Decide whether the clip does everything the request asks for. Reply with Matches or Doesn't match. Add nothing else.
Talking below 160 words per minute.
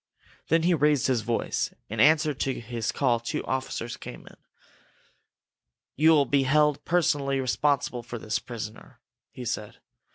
Matches